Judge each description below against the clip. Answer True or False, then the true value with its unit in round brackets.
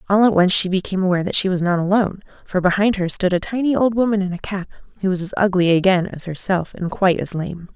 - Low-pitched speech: False (190 Hz)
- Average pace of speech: False (255 wpm)